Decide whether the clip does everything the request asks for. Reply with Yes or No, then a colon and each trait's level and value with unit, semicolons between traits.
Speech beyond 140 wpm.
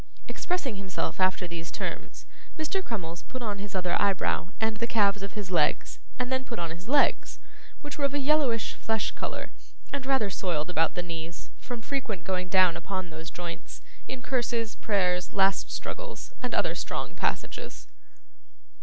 Yes: average, 170 wpm